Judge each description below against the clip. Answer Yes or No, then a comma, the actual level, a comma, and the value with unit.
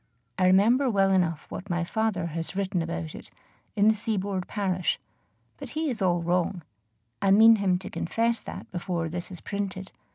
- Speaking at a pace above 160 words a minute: Yes, average, 175 wpm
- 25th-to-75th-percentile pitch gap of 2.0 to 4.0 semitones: Yes, average, 2.8 semitones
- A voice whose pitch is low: No, high, 190 Hz